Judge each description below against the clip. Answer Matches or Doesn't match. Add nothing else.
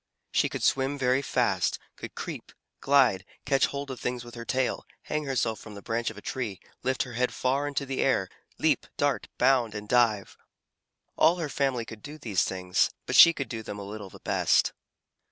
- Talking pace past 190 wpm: Matches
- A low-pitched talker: Matches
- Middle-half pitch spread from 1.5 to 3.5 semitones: Doesn't match